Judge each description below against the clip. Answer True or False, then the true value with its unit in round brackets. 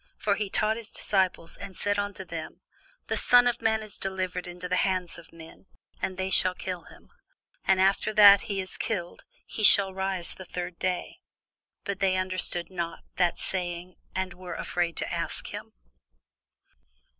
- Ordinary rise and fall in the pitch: False (2.1 semitones)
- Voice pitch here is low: False (185 Hz)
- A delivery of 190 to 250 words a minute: False (170 wpm)